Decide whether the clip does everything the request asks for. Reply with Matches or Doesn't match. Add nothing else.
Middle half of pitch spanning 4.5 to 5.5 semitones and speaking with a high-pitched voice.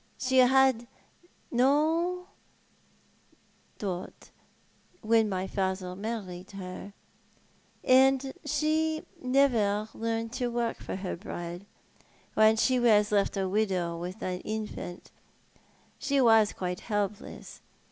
Matches